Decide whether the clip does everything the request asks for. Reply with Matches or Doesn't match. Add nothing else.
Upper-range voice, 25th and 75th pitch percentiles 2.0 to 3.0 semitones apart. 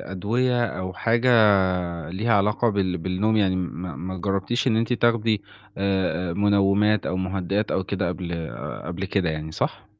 Doesn't match